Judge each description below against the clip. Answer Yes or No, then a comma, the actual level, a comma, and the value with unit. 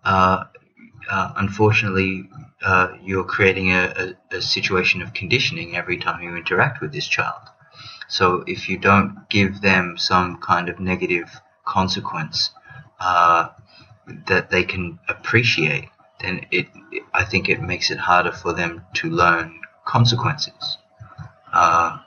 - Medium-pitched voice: No, very low, 95 Hz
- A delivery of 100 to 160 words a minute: Yes, slow, 135 wpm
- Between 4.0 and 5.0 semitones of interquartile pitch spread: No, average, 3.1 semitones